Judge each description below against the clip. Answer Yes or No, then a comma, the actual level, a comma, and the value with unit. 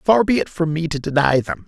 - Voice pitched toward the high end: No, medium, 160 Hz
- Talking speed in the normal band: No, fast, 285 wpm